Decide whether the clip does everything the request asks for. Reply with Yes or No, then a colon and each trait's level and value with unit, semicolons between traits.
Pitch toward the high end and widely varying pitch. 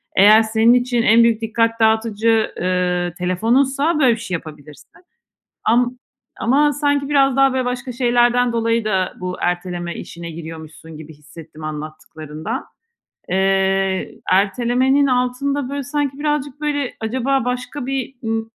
Yes: high, 230 Hz; wide, 6.1 semitones